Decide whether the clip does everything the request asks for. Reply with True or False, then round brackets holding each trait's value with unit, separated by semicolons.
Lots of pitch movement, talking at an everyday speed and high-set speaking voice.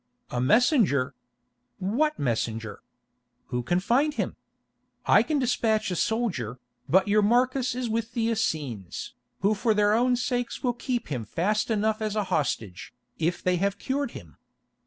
True (7.6 semitones; 155 wpm; 210 Hz)